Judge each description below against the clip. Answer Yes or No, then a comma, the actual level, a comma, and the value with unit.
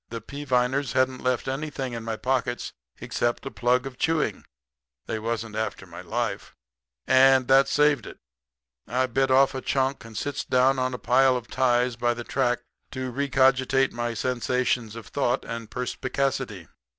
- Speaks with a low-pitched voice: Yes, low, 130 Hz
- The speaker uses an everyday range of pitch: No, narrow, 1.9 semitones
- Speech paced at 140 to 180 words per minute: Yes, average, 165 wpm